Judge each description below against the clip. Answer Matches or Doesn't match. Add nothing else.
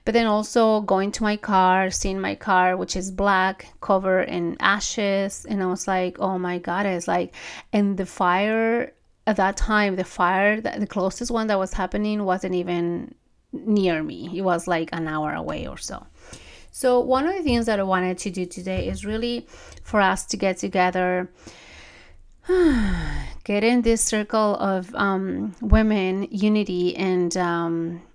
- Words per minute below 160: Doesn't match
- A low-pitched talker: Doesn't match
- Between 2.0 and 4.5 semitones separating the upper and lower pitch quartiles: Matches